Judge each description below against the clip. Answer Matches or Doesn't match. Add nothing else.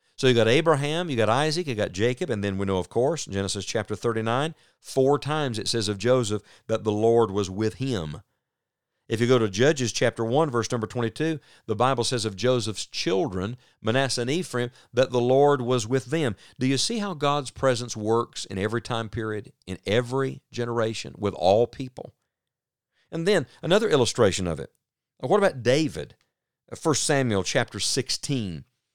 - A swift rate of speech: Doesn't match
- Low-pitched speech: Matches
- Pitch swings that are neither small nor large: Matches